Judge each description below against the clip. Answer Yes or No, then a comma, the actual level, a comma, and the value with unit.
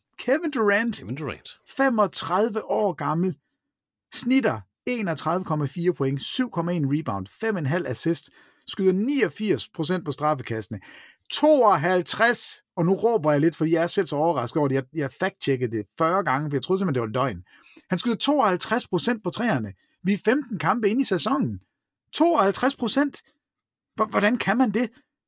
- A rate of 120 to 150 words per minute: Yes, slow, 145 wpm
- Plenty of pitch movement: Yes, wide, 7.1 semitones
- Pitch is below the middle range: No, medium, 185 Hz